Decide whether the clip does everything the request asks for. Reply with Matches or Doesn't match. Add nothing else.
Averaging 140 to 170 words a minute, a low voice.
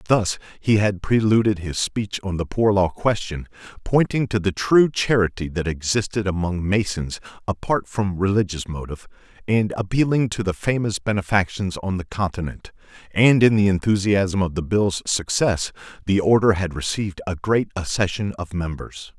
Matches